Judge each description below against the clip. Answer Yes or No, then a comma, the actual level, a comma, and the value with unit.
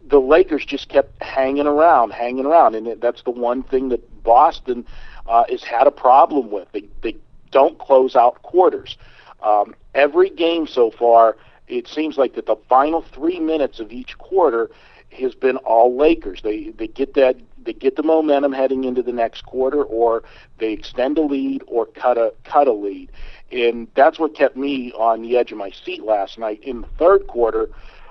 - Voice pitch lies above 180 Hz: No, low, 135 Hz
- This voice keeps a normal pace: Yes, average, 190 wpm